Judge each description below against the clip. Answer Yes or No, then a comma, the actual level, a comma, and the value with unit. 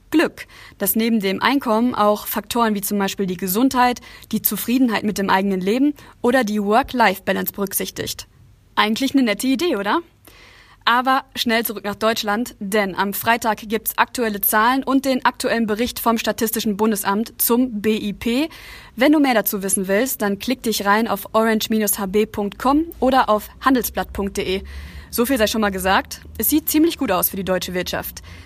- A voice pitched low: No, high, 215 Hz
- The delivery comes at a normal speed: Yes, average, 165 wpm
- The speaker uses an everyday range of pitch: Yes, average, 3.7 semitones